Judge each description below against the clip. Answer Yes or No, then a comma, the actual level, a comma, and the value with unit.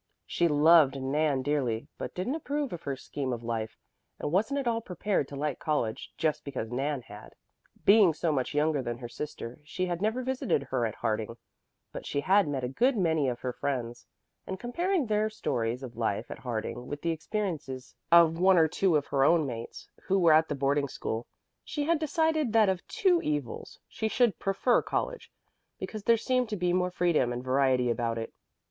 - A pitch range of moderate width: No, wide, 7.9 semitones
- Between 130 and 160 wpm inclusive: No, average, 200 wpm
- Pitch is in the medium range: Yes, medium, 150 Hz